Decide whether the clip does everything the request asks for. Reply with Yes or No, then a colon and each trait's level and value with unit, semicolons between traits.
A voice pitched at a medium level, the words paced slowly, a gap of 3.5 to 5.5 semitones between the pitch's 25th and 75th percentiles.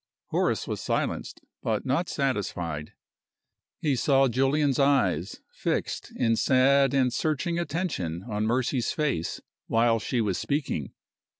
No: low, 130 Hz; slow, 120 wpm; average, 4.6 semitones